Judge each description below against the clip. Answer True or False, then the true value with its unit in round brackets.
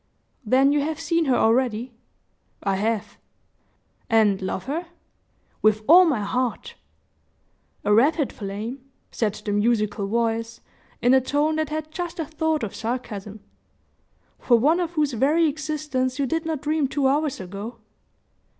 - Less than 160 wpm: True (145 wpm)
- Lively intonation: True (5.9 semitones)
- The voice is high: True (260 Hz)